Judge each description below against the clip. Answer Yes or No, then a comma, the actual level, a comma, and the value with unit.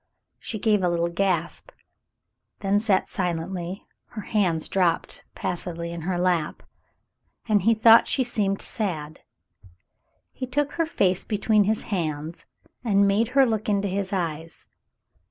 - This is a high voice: Yes, high, 195 Hz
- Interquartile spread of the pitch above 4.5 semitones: No, average, 4.0 semitones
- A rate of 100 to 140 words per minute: Yes, slow, 135 wpm